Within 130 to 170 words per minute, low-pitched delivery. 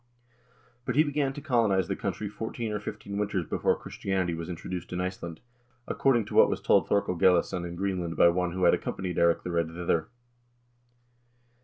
No: average, 185 wpm; very low, 90 Hz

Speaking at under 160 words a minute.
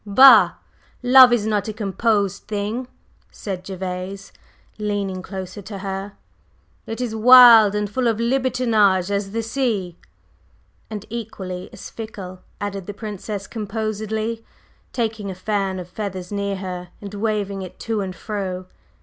Yes: average, 140 wpm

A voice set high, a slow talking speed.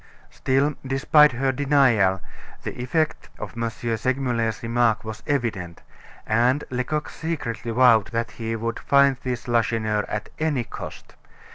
No: low, 120 Hz; slow, 130 wpm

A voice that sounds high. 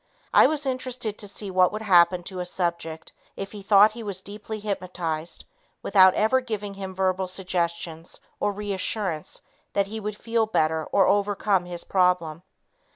Yes: high, 195 Hz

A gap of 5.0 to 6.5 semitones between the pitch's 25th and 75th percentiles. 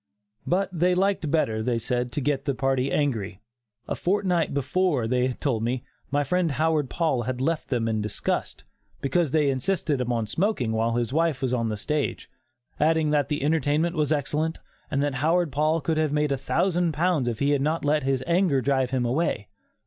No: average, 4.3 semitones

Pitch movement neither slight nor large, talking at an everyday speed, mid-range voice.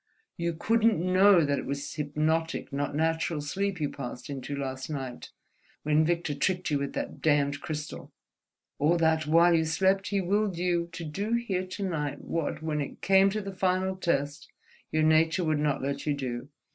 Yes: average, 4.1 semitones; average, 185 wpm; medium, 160 Hz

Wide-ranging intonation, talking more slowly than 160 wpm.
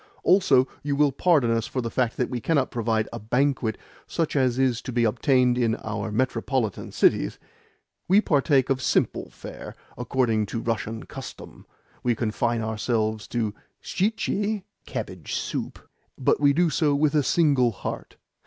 No: average, 4.0 semitones; average, 150 wpm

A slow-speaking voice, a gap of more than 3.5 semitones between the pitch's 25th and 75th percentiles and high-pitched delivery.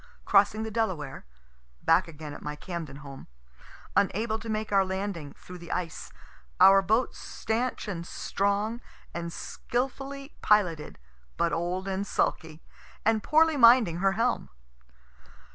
Yes: slow, 130 wpm; average, 4.7 semitones; high, 195 Hz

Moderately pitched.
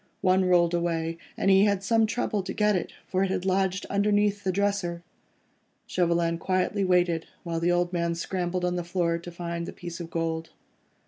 Yes: medium, 180 Hz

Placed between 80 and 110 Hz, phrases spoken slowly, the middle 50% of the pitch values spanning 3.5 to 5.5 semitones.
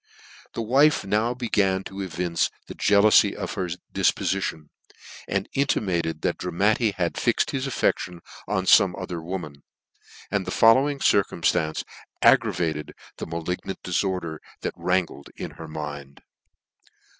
Yes: very low, 95 Hz; slow, 130 wpm; average, 3.9 semitones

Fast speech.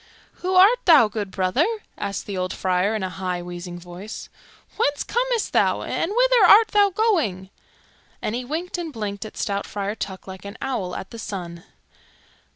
No: average, 175 wpm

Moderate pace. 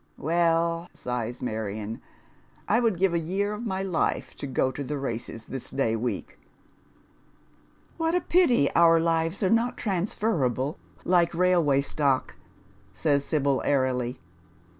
Yes: average, 145 wpm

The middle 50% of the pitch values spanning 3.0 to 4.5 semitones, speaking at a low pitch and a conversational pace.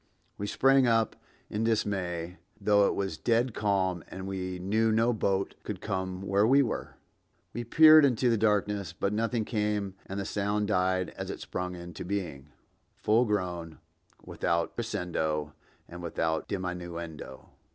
Yes: average, 3.6 semitones; low, 100 Hz; average, 150 wpm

